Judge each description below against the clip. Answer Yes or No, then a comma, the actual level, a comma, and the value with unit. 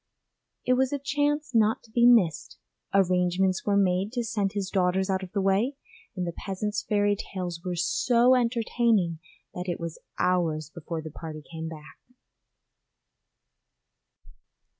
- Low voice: No, high, 190 Hz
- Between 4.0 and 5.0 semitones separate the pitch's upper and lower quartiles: Yes, average, 4.4 semitones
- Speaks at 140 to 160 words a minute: Yes, average, 145 wpm